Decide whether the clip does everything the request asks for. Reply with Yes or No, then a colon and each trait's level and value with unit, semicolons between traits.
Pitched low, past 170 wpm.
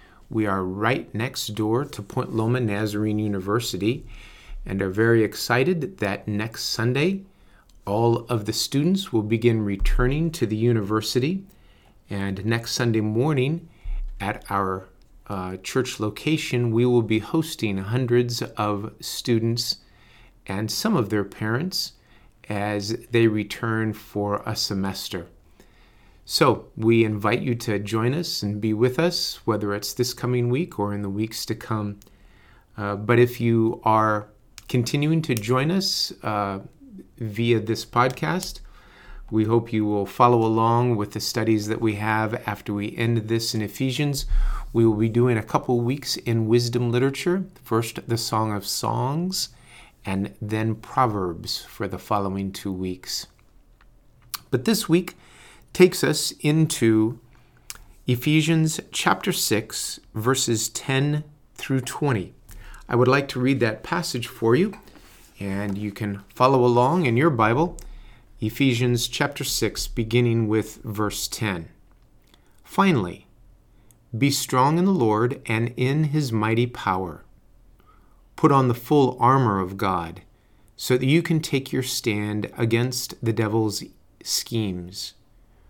No: low, 115 Hz; slow, 135 wpm